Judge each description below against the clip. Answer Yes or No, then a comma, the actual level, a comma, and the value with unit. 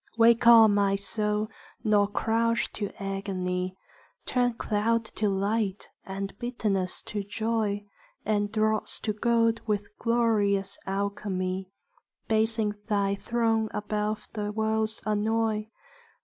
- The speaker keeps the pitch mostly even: Yes, narrow, 1.9 semitones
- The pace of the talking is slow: Yes, slow, 110 wpm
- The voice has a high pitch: Yes, high, 210 Hz